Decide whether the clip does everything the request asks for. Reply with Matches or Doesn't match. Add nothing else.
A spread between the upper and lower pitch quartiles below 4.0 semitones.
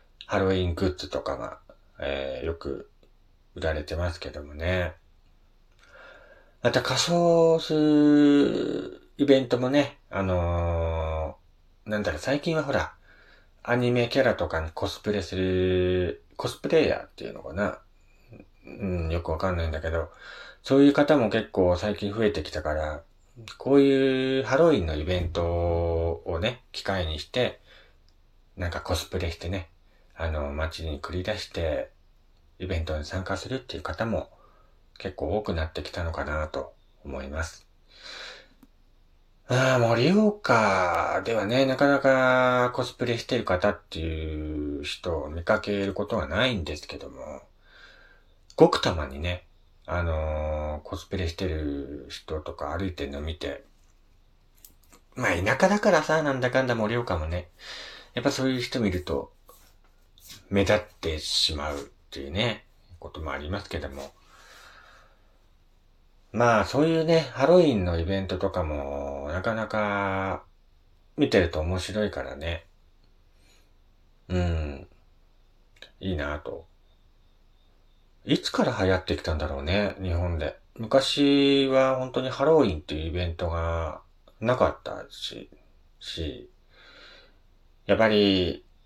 Doesn't match